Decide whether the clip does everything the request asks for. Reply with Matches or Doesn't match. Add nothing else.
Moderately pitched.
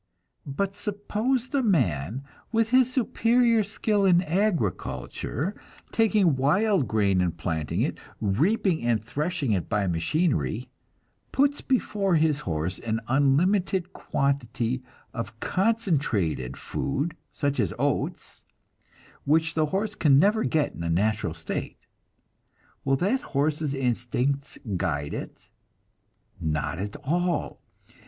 Matches